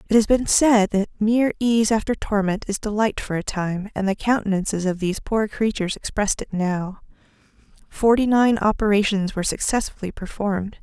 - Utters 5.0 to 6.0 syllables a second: Yes, 5.5 syllables/s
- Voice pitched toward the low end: No, high, 210 Hz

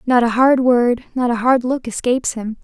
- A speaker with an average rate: No, fast, 230 wpm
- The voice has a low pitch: No, high, 245 Hz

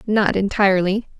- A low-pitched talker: No, high, 195 Hz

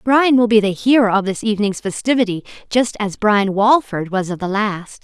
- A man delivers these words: No, female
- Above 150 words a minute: Yes, fast, 205 wpm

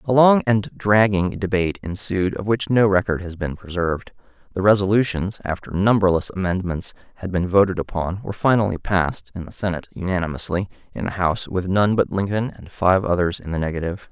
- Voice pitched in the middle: No, very low, 95 Hz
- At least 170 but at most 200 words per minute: Yes, average, 180 wpm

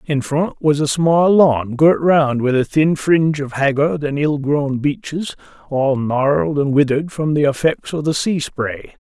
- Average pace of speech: Yes, average, 190 wpm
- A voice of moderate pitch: Yes, medium, 145 Hz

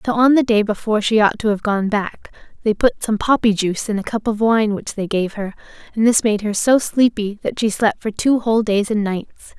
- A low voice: No, high, 215 Hz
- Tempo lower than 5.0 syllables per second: No, 5.5 syllables/s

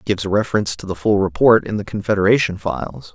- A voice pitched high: No, very low, 95 Hz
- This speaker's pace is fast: No, average, 190 wpm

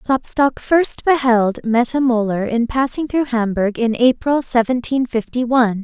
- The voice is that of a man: No, female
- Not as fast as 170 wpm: Yes, average, 145 wpm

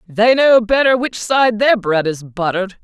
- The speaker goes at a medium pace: Yes, average, 190 wpm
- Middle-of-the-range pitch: No, high, 215 Hz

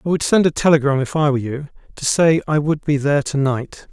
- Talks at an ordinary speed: No, fast, 260 wpm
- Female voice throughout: No, male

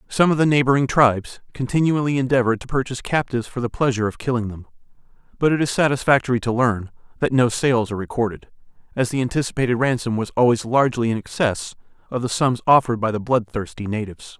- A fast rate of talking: No, average, 185 wpm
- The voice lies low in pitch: Yes, low, 125 Hz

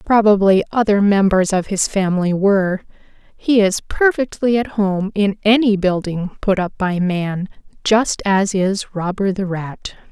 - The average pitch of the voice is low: No, high, 200 Hz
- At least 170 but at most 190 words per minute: No, average, 150 wpm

